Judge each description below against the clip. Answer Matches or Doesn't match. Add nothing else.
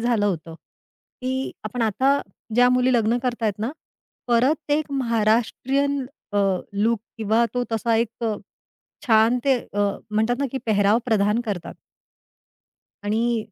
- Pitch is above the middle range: Matches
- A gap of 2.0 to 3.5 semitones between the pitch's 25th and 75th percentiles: Matches